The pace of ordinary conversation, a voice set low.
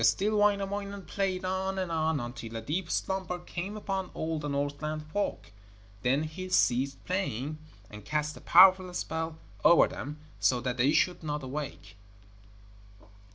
No: average, 150 wpm; medium, 160 Hz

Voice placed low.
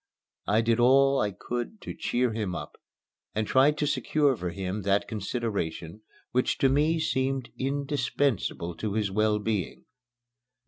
Yes: low, 115 Hz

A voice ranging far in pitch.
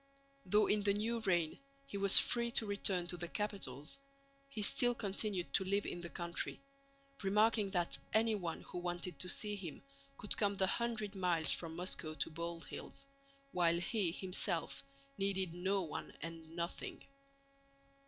No: average, 3.3 semitones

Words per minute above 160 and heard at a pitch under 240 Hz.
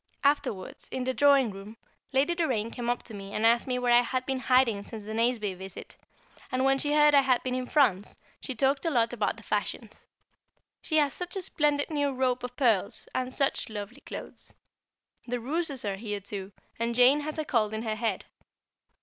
No: fast, 205 wpm; very high, 250 Hz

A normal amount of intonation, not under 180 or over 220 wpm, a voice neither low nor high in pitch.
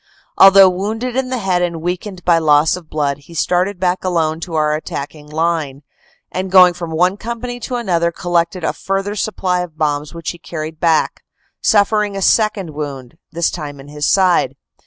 Yes: average, 3.7 semitones; average, 190 wpm; medium, 175 Hz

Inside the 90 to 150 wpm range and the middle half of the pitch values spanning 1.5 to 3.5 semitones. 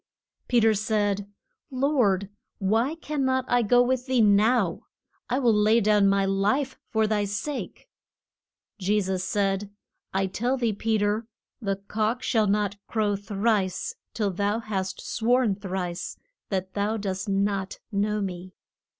Yes: average, 145 wpm; average, 2.9 semitones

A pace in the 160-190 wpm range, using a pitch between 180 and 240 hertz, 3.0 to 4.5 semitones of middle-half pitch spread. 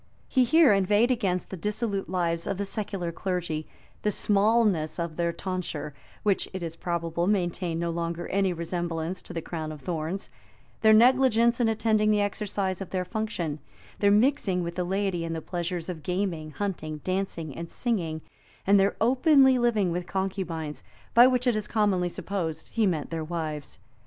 Yes: average, 170 wpm; medium, 185 Hz; average, 3.9 semitones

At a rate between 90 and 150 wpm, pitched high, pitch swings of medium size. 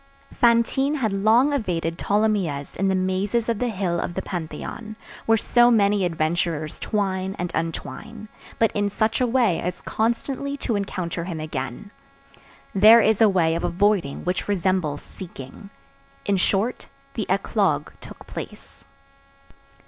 Yes: average, 140 wpm; high, 195 Hz; average, 4.5 semitones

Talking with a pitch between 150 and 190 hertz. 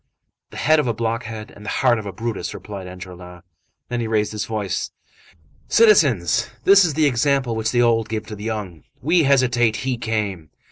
No: low, 115 Hz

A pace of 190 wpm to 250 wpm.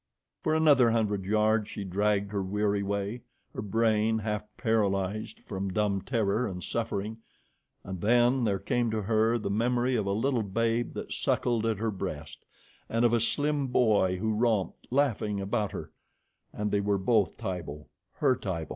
No: average, 165 wpm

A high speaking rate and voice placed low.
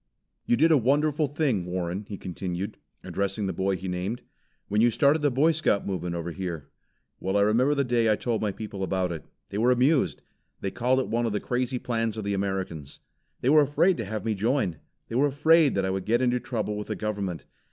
Yes: fast, 225 wpm; low, 110 Hz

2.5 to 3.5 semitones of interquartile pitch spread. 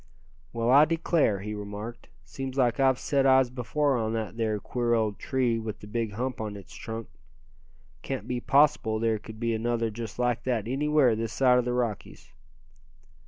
Yes: average, 2.9 semitones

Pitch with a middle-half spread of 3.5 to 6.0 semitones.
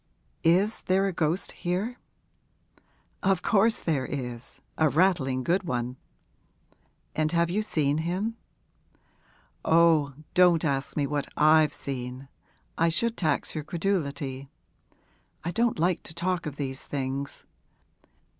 Yes: average, 4.6 semitones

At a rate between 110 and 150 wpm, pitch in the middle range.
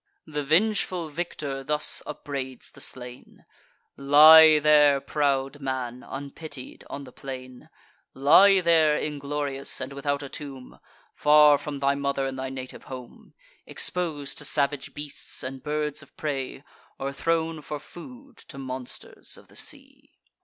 Yes: average, 140 wpm; medium, 145 Hz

